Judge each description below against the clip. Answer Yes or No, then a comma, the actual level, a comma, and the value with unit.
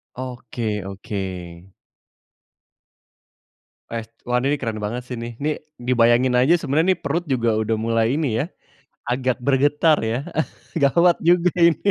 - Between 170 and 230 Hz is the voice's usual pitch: No, low, 125 Hz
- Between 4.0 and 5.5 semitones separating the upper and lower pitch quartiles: Yes, average, 4.3 semitones